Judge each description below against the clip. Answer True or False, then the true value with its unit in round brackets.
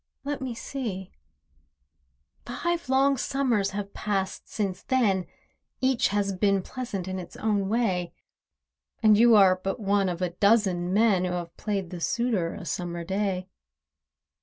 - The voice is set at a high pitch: True (200 Hz)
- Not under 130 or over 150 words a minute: True (145 wpm)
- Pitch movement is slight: False (4.1 semitones)